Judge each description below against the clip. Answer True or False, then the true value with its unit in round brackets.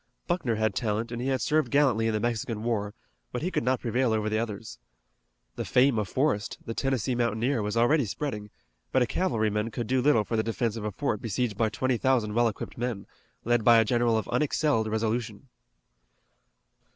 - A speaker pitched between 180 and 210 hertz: False (115 Hz)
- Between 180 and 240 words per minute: True (200 wpm)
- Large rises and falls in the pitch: False (2.9 semitones)